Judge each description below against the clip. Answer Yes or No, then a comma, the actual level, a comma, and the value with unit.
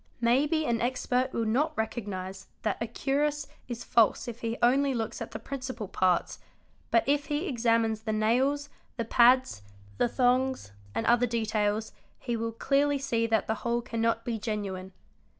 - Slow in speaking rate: No, average, 170 wpm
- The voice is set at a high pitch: Yes, high, 235 Hz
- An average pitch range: Yes, average, 3.0 semitones